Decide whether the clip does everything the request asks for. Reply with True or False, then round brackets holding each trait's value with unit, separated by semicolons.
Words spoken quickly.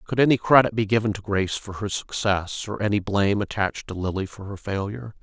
True (220 wpm)